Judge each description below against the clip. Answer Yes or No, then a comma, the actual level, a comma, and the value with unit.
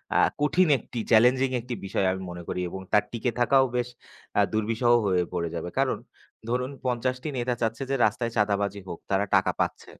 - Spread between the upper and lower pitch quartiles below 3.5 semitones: No, average, 4.0 semitones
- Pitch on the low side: Yes, low, 115 Hz